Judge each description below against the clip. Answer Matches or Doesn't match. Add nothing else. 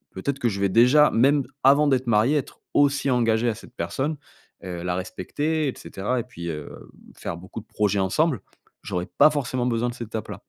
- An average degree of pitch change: Doesn't match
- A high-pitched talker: Doesn't match